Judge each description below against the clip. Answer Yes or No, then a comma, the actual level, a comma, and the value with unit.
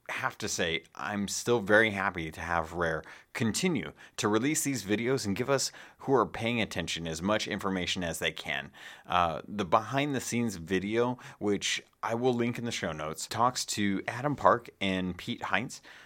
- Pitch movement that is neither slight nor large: Yes, average, 4.3 semitones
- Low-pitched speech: Yes, low, 105 Hz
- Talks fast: No, average, 185 wpm